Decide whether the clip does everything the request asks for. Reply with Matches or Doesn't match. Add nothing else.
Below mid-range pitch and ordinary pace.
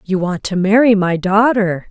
Doesn't match